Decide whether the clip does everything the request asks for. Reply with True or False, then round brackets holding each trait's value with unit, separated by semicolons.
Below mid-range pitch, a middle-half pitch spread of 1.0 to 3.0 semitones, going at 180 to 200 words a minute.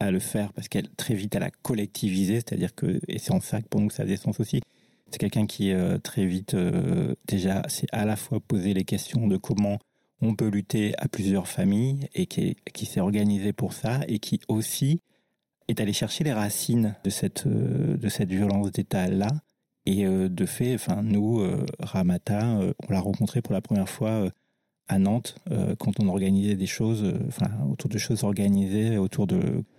True (105 Hz; 2.7 semitones; 190 wpm)